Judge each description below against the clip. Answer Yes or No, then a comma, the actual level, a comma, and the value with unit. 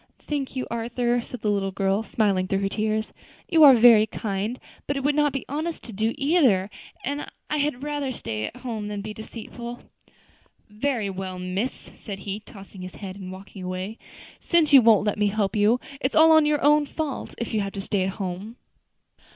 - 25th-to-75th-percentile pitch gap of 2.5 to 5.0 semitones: No, wide, 5.5 semitones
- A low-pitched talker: No, high, 220 Hz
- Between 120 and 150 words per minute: No, average, 200 wpm